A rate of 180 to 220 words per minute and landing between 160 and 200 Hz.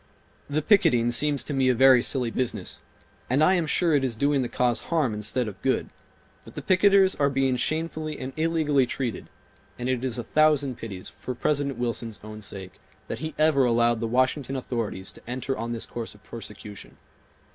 No: average, 190 wpm; low, 130 Hz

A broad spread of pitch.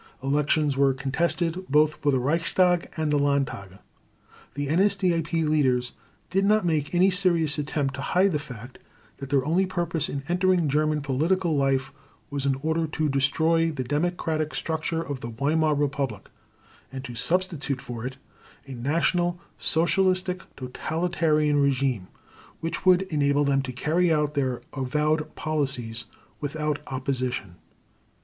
No: average, 3.4 semitones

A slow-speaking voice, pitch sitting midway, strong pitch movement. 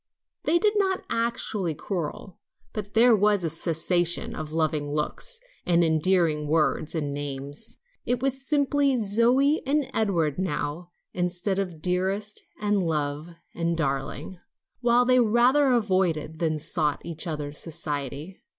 Yes: slow, 130 wpm; medium, 180 Hz; wide, 6.8 semitones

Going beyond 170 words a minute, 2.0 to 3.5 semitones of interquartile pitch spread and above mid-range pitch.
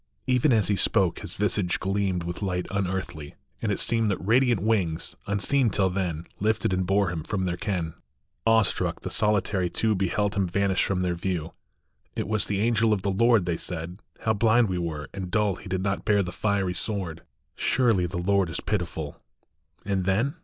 No: average, 200 wpm; average, 2.9 semitones; very low, 95 Hz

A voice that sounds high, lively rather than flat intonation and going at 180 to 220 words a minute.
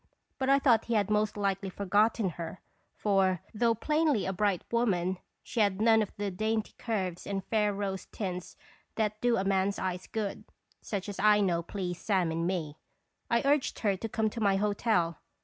No: high, 205 Hz; average, 2.8 semitones; average, 185 wpm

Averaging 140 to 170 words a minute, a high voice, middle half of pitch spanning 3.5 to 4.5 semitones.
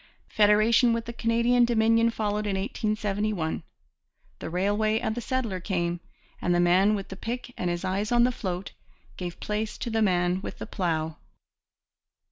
Yes: average, 165 wpm; high, 210 Hz; average, 3.8 semitones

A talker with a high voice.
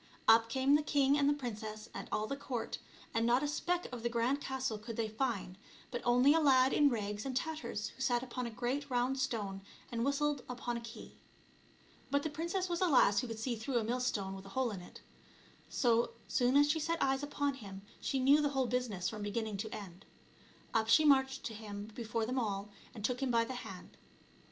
Yes: high, 245 Hz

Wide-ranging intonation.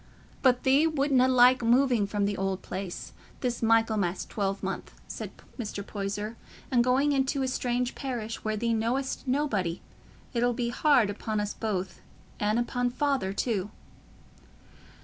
No: average, 3.8 semitones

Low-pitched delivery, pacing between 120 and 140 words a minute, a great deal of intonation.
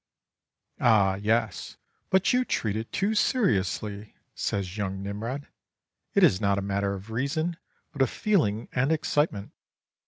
Yes: low, 110 Hz; slow, 135 wpm; wide, 6.7 semitones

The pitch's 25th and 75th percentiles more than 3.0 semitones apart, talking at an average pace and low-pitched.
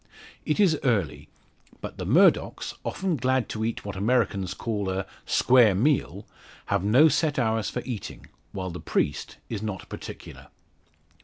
Yes: average, 4.9 semitones; average, 150 wpm; low, 110 Hz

